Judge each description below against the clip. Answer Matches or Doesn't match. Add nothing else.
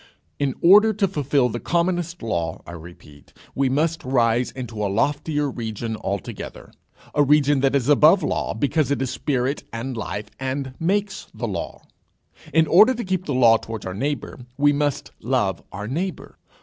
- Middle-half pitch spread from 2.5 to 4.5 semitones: Doesn't match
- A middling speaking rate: Matches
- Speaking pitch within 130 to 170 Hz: Matches